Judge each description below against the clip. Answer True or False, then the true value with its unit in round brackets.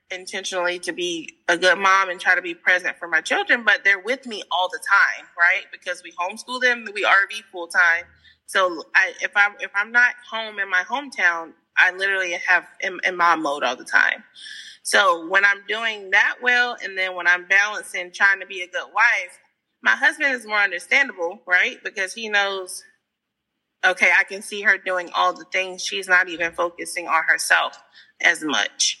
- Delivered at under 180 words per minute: False (190 wpm)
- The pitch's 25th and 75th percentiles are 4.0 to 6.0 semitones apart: False (3.5 semitones)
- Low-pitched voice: False (195 Hz)